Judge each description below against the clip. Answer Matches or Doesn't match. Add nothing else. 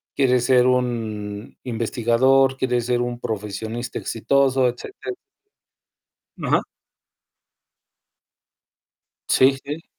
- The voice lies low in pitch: Matches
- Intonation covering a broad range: Doesn't match